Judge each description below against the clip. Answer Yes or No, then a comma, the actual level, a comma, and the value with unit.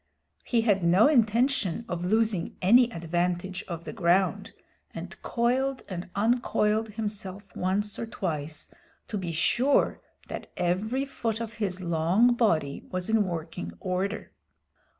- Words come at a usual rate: No, slow, 130 wpm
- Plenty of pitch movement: No, average, 4.5 semitones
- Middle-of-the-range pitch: No, high, 200 Hz